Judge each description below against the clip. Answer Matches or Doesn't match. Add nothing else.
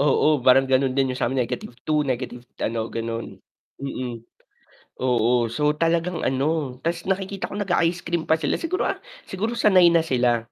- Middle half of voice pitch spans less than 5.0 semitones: Doesn't match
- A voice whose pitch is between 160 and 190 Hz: Doesn't match